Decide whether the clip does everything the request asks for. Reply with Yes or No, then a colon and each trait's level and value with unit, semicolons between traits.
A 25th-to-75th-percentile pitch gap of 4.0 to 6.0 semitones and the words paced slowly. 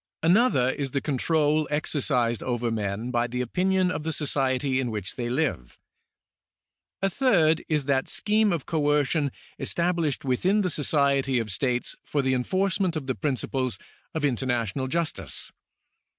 No: average, 4.4 semitones; average, 145 wpm